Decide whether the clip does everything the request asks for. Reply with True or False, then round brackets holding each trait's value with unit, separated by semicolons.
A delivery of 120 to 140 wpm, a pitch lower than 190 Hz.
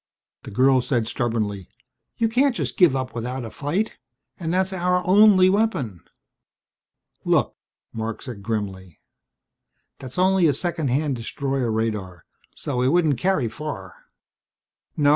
True (135 wpm; 135 Hz)